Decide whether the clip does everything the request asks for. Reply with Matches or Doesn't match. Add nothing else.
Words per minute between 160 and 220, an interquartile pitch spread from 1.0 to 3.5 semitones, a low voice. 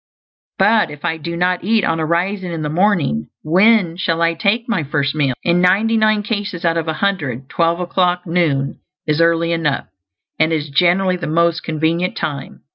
Doesn't match